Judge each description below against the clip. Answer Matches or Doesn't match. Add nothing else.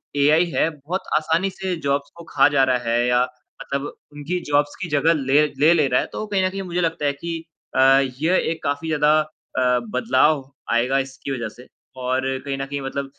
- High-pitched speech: Doesn't match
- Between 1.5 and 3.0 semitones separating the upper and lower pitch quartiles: Doesn't match